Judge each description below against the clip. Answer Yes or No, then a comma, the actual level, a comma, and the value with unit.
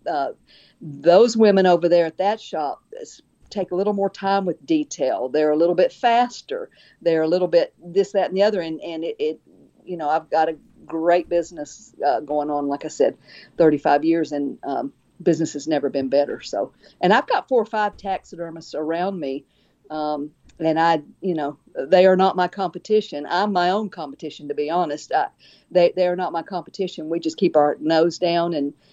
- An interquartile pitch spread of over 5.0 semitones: No, average, 3.8 semitones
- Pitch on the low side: No, medium, 175 Hz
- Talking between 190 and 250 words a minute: Yes, average, 200 wpm